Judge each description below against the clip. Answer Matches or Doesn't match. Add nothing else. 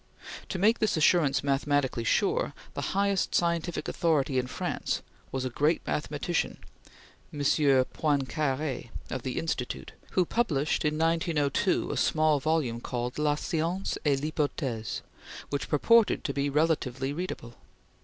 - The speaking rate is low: Matches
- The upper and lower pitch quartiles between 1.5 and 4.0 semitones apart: Matches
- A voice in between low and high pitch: Matches